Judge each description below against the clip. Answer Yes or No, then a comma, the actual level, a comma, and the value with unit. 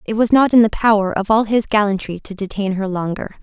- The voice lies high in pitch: Yes, high, 210 Hz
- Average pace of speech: No, fast, 245 wpm